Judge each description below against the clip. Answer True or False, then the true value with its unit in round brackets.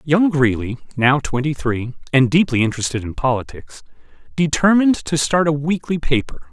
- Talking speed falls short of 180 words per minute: True (145 wpm)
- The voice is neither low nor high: True (145 Hz)